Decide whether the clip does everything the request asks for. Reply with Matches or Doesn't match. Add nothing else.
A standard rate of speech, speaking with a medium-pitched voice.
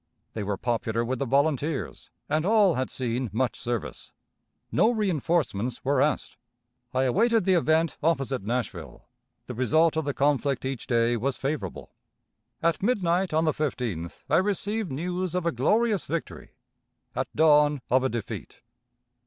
Matches